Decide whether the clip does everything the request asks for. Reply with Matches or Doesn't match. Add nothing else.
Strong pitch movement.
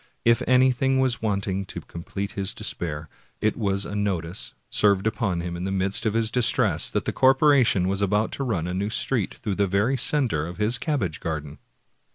Doesn't match